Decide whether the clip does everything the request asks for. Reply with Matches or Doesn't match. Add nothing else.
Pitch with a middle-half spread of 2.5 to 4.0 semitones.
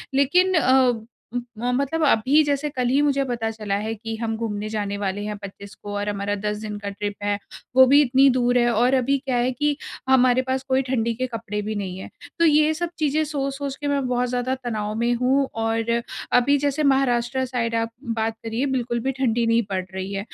Matches